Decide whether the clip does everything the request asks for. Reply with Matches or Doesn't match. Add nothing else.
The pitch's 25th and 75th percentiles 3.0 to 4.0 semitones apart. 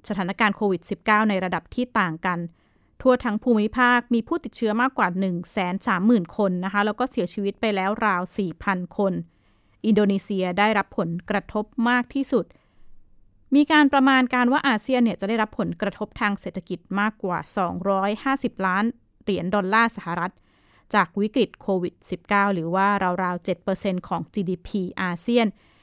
Matches